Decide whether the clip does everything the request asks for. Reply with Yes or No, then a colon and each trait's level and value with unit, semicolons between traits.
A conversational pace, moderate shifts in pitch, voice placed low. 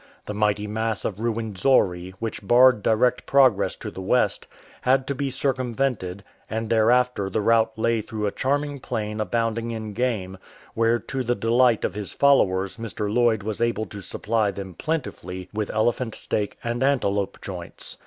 Yes: average, 165 wpm; average, 3.1 semitones; low, 110 Hz